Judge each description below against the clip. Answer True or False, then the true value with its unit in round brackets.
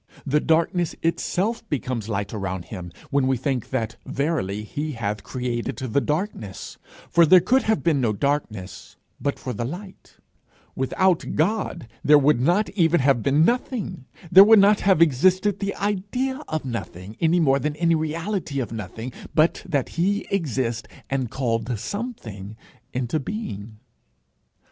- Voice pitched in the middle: True (145 Hz)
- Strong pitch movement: True (7.6 semitones)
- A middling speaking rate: True (150 wpm)